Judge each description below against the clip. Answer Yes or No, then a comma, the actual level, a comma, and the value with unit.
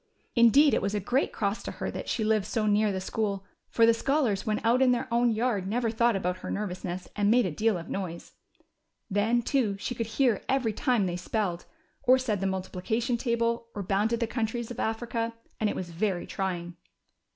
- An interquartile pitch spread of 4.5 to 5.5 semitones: No, average, 3.3 semitones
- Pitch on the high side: Yes, high, 220 Hz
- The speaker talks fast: Yes, fast, 210 wpm